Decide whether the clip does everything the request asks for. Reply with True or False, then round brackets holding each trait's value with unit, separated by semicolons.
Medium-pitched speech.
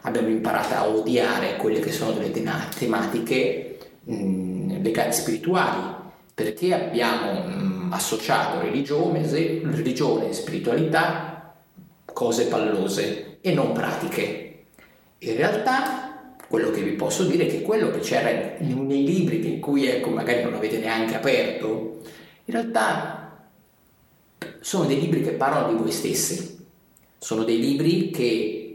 True (155 Hz)